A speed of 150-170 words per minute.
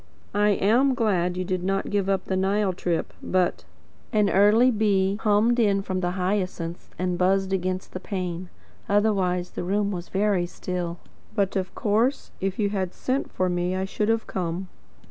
No: average, 180 wpm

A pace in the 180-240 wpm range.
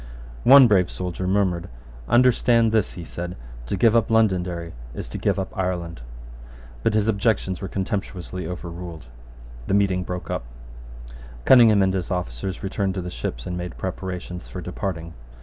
No: average, 155 wpm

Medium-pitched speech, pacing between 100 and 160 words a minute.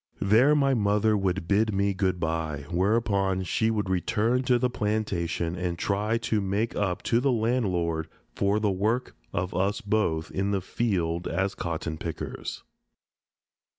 No: low, 100 Hz; average, 150 wpm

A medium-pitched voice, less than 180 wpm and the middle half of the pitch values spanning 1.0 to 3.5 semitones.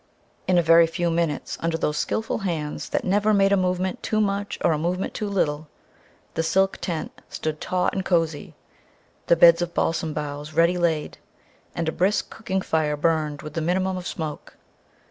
No: medium, 170 Hz; average, 185 wpm; average, 3.0 semitones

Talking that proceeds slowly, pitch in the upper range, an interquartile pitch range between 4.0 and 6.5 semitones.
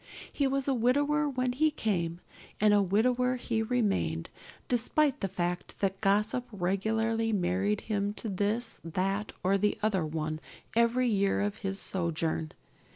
No: average, 150 wpm; high, 210 Hz; average, 4.5 semitones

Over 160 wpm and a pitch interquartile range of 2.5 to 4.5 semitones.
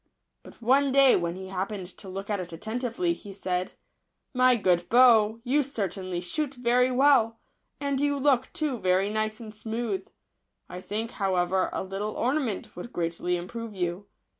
No: average, 170 wpm; average, 5.2 semitones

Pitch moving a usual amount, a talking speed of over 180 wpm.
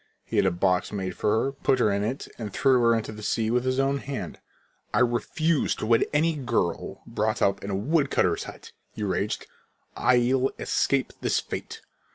Yes: average, 4.4 semitones; average, 195 wpm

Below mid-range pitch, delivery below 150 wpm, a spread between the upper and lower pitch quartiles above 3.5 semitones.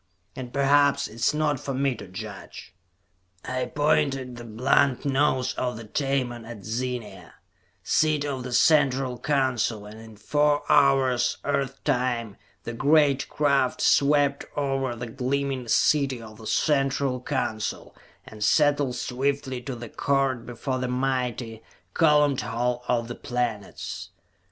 No: low, 130 Hz; slow, 135 wpm; average, 2.7 semitones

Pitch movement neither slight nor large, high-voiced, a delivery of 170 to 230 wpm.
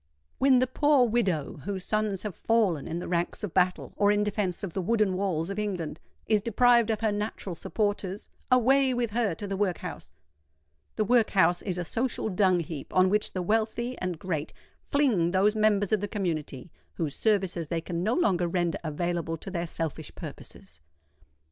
Yes: average, 3.8 semitones; high, 195 Hz; average, 180 wpm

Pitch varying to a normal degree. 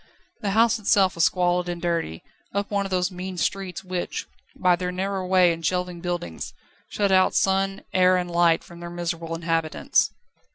No: narrow, 1.8 semitones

